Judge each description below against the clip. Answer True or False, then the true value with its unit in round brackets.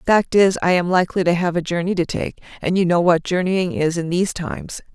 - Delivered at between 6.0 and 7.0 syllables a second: True (6.1 syllables/s)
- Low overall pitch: False (175 Hz)